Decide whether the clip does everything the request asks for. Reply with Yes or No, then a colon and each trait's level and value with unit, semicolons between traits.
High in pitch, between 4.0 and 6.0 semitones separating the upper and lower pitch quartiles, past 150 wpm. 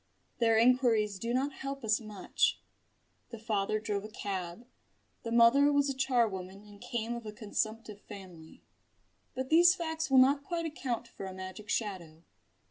Yes: high, 230 Hz; average, 4.3 semitones; average, 160 wpm